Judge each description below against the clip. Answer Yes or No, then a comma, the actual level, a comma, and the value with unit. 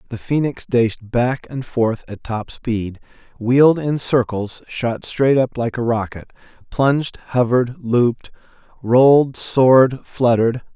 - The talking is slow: Yes, slow, 125 wpm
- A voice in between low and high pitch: No, low, 125 Hz